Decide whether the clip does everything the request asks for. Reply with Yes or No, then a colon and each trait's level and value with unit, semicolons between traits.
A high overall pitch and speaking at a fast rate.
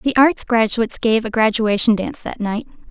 No: high, 230 Hz; average, 185 wpm